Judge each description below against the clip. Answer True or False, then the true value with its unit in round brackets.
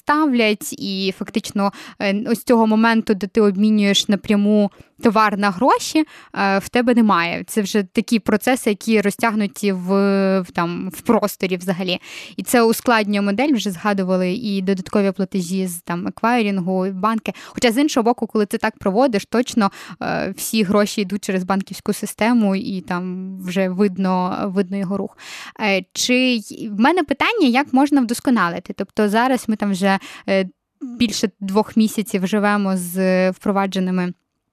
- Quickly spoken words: False (140 wpm)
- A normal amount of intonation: True (3.0 semitones)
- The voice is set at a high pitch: True (205 Hz)